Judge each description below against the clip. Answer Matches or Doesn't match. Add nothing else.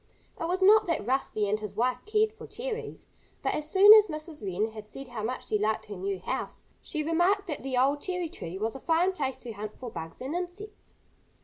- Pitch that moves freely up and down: Matches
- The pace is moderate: Doesn't match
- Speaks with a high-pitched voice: Matches